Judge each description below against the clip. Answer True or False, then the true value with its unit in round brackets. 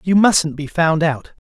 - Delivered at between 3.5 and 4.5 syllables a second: True (3.9 syllables/s)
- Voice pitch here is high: False (165 Hz)